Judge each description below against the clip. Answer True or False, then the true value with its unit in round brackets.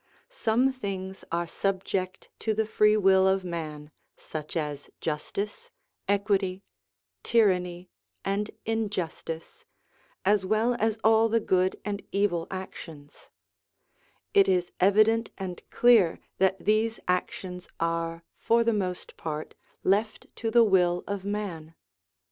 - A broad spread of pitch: False (3.4 semitones)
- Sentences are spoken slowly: True (120 wpm)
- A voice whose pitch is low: False (195 Hz)